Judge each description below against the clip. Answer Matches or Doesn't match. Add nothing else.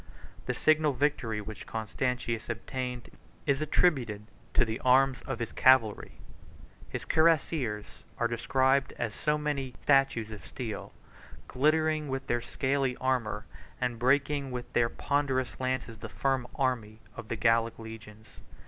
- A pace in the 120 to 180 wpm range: Matches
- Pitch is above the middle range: Doesn't match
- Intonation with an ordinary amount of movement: Matches